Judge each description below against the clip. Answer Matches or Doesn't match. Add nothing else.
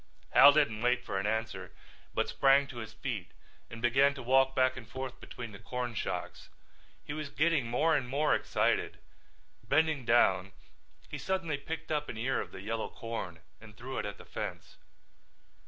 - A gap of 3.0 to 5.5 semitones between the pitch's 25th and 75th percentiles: Matches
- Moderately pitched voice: Doesn't match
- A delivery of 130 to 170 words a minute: Doesn't match